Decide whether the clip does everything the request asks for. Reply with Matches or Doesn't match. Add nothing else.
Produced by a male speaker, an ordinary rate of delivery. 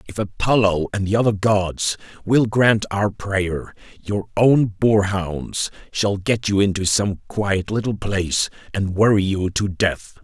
Matches